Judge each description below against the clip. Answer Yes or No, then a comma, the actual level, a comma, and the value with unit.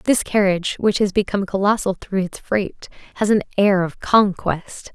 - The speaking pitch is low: No, high, 195 Hz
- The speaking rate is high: No, average, 170 wpm